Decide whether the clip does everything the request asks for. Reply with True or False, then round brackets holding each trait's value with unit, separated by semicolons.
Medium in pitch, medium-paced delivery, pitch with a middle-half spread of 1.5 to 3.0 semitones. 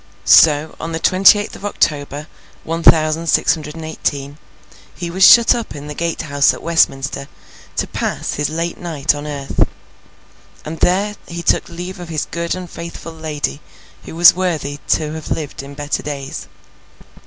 True (160 Hz; 175 wpm; 2.5 semitones)